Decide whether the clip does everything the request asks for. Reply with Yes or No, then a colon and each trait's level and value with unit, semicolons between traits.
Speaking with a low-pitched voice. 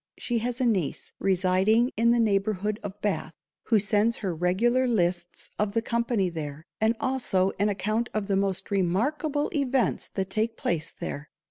No: high, 210 Hz